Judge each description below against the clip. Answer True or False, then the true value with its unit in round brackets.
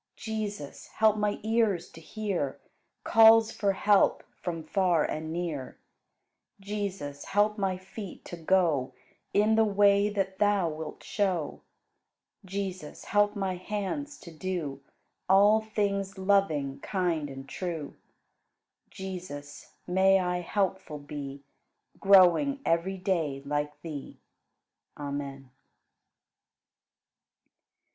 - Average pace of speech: False (105 wpm)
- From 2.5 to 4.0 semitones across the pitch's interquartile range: False (4.6 semitones)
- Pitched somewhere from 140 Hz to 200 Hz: True (190 Hz)